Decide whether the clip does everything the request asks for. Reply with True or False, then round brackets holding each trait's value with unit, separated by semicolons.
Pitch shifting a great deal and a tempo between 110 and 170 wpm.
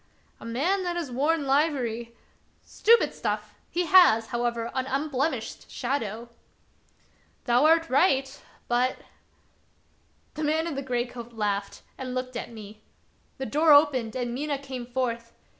False (4.0 semitones; 155 wpm)